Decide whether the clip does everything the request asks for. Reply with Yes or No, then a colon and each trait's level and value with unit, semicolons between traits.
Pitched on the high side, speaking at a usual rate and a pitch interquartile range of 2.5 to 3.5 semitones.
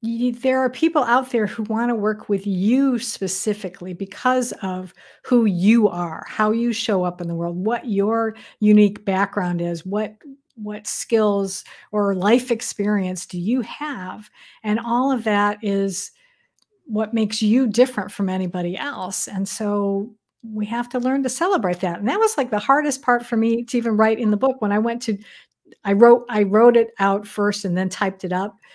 Yes: high, 215 Hz; average, 190 wpm; average, 3.2 semitones